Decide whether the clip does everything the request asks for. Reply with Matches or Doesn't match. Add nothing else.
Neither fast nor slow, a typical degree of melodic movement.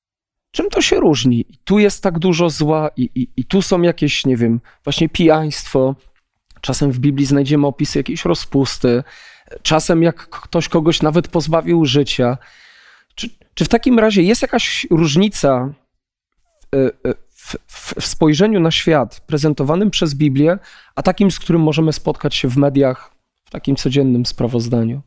Matches